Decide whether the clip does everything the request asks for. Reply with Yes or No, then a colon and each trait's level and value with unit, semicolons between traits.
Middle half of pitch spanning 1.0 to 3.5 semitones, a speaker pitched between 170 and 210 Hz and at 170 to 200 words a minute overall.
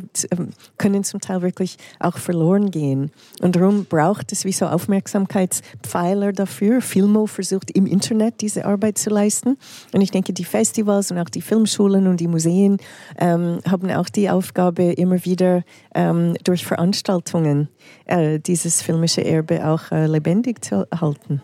No: average, 2.8 semitones; medium, 185 Hz; average, 150 wpm